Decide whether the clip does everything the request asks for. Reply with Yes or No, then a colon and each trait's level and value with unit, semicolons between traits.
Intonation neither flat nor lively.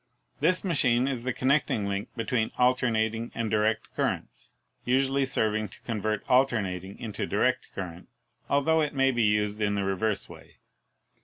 Yes: average, 3.8 semitones